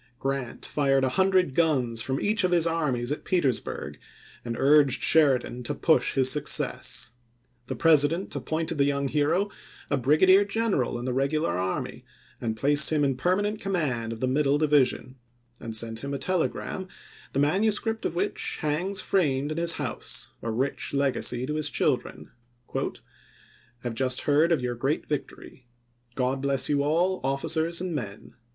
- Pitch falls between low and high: Yes, medium, 145 Hz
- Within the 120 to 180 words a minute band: Yes, average, 165 wpm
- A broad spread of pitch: No, average, 4.3 semitones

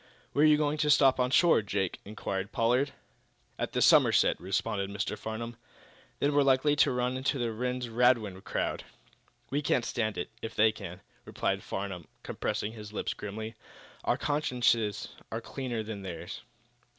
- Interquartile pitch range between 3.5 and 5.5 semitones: Yes, average, 4.0 semitones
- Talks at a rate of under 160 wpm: No, average, 165 wpm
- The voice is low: Yes, low, 115 Hz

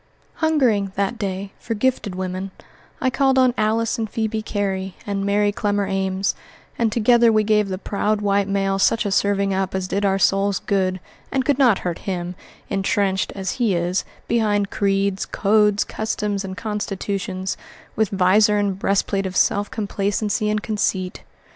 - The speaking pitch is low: No, high, 200 Hz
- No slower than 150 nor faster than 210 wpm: Yes, average, 160 wpm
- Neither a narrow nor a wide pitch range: No, narrow, 1.9 semitones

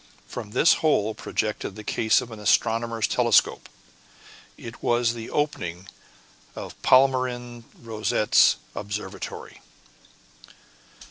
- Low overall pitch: Yes, low, 115 Hz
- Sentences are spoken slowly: Yes, slow, 95 wpm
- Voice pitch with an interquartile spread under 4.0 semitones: Yes, narrow, 2.4 semitones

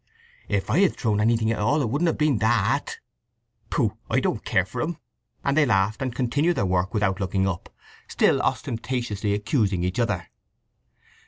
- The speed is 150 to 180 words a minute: Yes, average, 175 wpm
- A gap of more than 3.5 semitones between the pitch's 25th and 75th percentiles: Yes, average, 5.3 semitones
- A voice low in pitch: Yes, low, 110 Hz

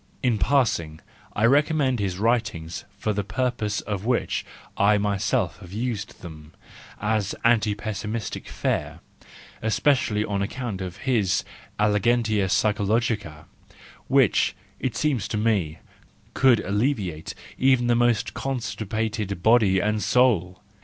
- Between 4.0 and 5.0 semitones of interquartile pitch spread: No, average, 3.3 semitones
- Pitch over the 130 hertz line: No, low, 105 Hz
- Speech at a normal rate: No, slow, 120 wpm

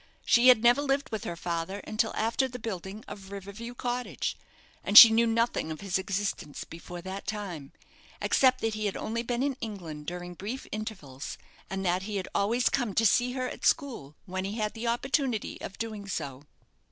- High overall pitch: Yes, high, 215 Hz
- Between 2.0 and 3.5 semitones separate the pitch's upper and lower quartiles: No, average, 4.0 semitones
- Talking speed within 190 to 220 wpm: Yes, average, 195 wpm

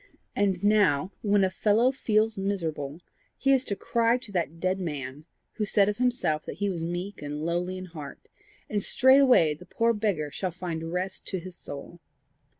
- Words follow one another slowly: No, average, 180 wpm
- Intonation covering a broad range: No, average, 4.3 semitones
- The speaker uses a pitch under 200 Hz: Yes, medium, 185 Hz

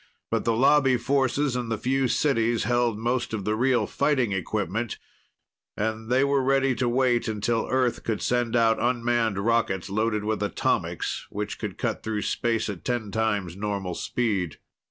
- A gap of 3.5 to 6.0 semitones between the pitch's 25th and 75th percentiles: No, average, 2.8 semitones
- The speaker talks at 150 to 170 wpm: Yes, average, 165 wpm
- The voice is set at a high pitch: No, low, 115 Hz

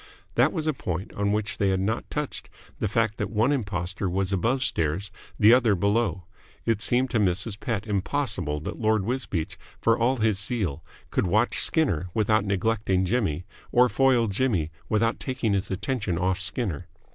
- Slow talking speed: No, average, 170 wpm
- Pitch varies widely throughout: No, average, 3.8 semitones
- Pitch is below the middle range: Yes, low, 105 Hz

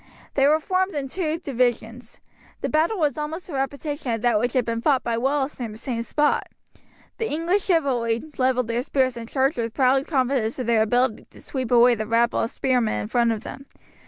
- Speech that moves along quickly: Yes, fast, 210 wpm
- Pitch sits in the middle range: No, very high, 255 Hz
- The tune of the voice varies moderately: Yes, average, 3.9 semitones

